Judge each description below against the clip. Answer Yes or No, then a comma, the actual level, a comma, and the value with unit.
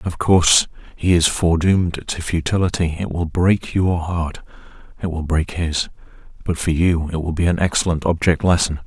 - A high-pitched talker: No, very low, 85 Hz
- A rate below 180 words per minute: Yes, average, 170 wpm